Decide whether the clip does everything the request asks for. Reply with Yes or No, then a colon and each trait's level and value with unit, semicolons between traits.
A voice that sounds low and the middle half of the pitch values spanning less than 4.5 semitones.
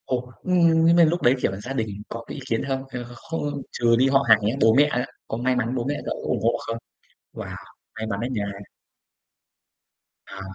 Yes: low, 125 Hz; average, 3.8 semitones